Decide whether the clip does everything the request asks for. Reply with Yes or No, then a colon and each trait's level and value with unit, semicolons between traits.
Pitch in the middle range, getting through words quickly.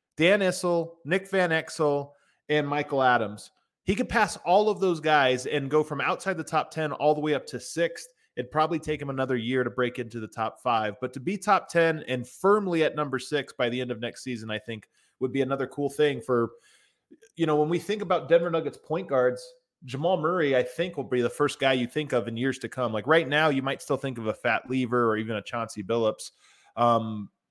Yes: medium, 145 Hz; fast, 235 wpm